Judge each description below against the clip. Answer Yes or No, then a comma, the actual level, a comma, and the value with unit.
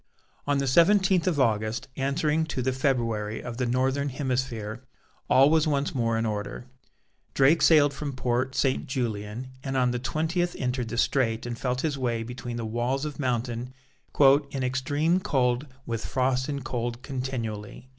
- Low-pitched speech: Yes, low, 130 Hz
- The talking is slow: No, average, 165 wpm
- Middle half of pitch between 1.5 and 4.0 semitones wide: Yes, average, 2.8 semitones